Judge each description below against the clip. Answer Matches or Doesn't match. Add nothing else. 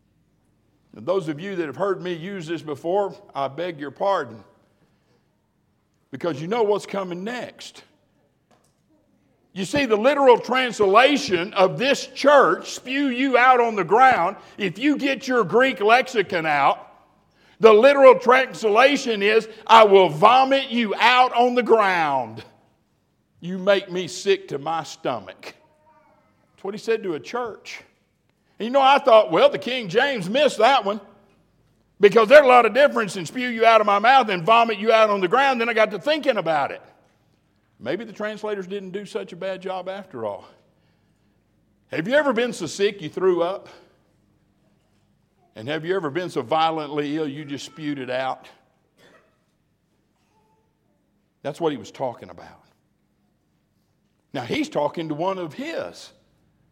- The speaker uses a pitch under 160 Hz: Doesn't match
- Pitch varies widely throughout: Matches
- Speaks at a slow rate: Doesn't match